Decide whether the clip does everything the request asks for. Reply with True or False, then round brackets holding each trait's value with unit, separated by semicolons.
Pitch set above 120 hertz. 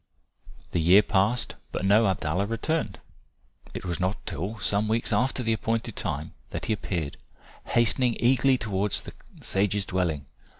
False (105 Hz)